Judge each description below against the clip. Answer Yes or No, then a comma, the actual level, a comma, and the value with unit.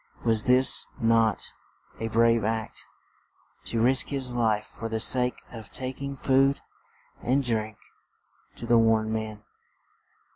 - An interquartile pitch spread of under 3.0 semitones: Yes, narrow, 2.4 semitones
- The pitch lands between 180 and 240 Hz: No, low, 115 Hz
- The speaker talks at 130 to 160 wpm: Yes, slow, 135 wpm